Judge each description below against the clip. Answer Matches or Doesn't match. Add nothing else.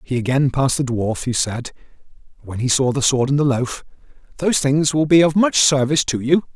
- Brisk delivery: Matches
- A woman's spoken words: Doesn't match